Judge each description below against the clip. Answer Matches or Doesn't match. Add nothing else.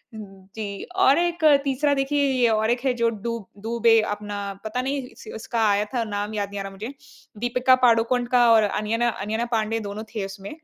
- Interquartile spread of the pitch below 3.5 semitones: Matches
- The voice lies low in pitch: Doesn't match